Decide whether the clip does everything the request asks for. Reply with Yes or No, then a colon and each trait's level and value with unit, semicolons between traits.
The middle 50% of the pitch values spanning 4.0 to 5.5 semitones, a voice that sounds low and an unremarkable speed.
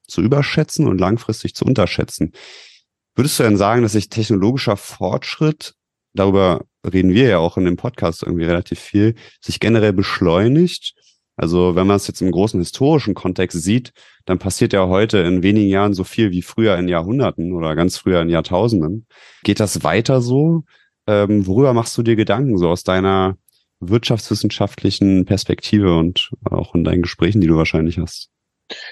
Yes: average, 4.3 semitones; low, 100 Hz; average, 165 wpm